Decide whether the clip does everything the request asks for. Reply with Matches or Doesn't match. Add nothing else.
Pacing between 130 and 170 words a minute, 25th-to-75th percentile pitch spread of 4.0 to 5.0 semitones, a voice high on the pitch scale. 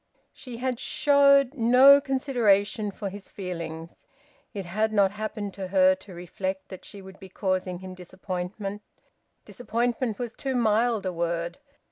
Matches